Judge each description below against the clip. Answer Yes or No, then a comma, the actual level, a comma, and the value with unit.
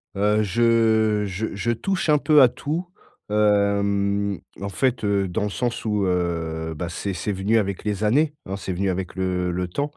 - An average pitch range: Yes, average, 3.2 semitones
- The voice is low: Yes, low, 100 Hz